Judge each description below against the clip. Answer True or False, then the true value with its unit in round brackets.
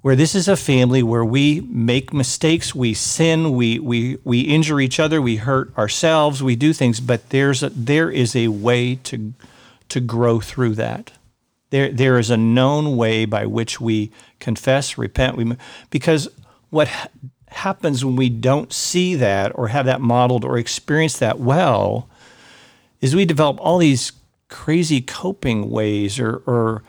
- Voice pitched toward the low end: True (130 Hz)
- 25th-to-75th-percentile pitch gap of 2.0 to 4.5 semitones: True (3.7 semitones)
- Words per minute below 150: False (165 wpm)